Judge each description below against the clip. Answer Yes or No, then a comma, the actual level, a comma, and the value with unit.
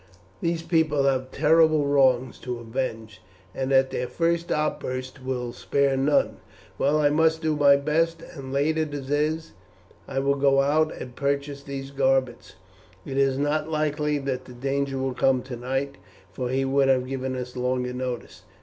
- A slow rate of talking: No, average, 170 wpm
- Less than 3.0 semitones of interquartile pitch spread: Yes, narrow, 2.4 semitones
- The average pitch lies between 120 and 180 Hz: Yes, low, 135 Hz